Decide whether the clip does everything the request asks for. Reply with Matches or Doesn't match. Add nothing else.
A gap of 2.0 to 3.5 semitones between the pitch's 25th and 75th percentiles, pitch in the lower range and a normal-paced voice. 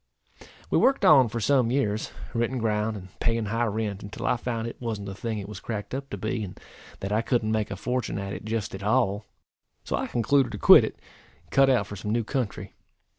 Doesn't match